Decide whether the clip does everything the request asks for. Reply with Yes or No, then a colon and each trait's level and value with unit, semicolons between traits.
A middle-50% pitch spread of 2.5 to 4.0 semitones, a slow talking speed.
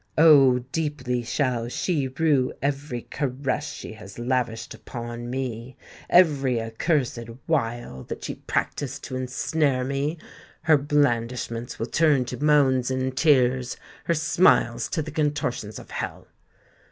Yes: average, 3.4 semitones; slow, 120 wpm